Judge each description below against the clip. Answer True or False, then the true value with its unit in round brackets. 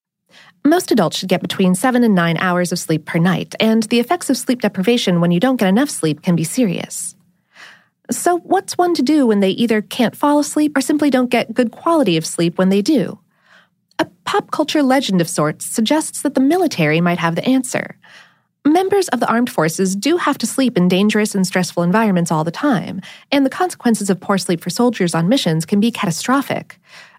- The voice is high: True (220 Hz)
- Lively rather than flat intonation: True (7.3 semitones)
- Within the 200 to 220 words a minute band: True (205 wpm)